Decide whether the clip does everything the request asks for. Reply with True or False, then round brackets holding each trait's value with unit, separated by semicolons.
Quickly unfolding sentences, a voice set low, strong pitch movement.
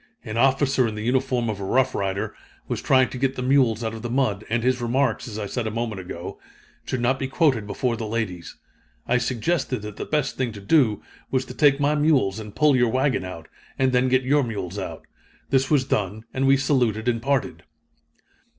False (215 wpm; 125 Hz; 3.5 semitones)